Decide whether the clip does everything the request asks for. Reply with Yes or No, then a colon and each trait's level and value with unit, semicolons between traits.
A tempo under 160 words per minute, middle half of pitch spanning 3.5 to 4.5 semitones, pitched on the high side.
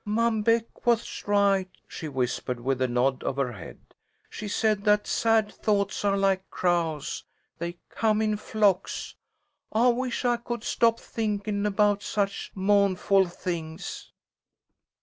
Yes: slow, 135 wpm; average, 3.8 semitones; high, 205 Hz